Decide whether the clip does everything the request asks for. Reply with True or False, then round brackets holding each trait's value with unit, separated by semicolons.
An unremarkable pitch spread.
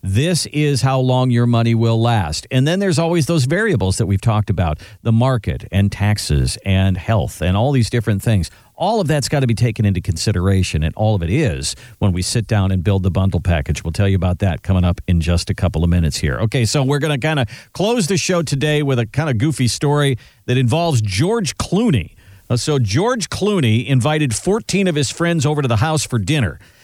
False (7.0 semitones)